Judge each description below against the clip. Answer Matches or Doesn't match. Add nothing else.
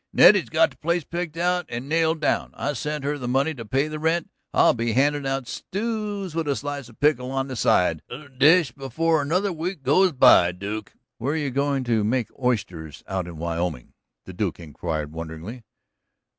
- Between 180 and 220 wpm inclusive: Matches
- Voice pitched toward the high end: Doesn't match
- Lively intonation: Matches